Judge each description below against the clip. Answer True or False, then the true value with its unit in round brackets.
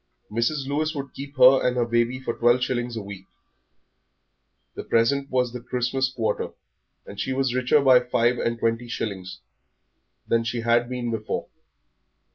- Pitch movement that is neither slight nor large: False (2.0 semitones)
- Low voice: True (120 Hz)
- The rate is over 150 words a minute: True (160 wpm)